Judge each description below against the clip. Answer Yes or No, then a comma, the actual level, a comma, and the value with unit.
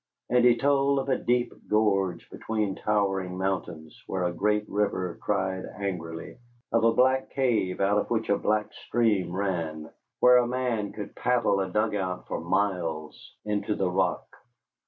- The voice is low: Yes, low, 105 Hz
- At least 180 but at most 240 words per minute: No, average, 155 wpm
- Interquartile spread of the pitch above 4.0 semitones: No, average, 3.7 semitones